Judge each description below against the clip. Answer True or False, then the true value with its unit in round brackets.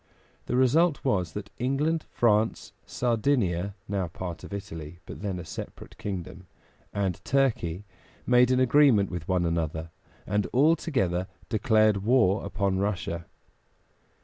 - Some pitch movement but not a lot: False (5.7 semitones)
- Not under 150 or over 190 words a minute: False (135 wpm)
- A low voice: True (100 Hz)